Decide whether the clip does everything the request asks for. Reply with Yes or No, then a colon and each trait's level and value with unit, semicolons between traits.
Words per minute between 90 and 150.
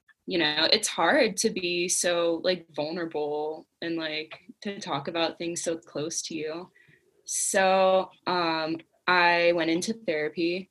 Yes: average, 140 wpm